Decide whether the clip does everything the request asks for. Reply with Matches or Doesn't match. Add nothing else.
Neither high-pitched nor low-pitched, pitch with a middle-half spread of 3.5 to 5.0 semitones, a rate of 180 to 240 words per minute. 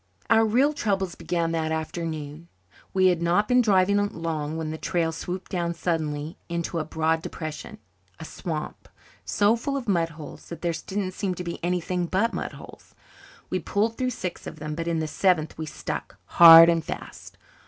Doesn't match